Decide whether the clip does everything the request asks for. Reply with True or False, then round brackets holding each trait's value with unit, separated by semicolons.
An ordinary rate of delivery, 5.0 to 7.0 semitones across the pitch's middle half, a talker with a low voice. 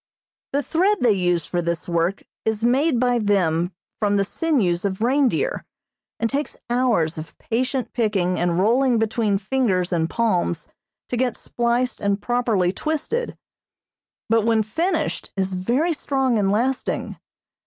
False (145 wpm; 5.5 semitones; 225 Hz)